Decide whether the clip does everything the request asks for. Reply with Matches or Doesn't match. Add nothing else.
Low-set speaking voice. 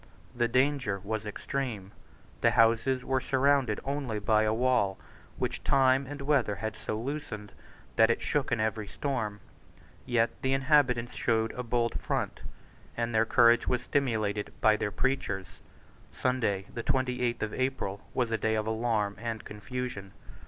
Matches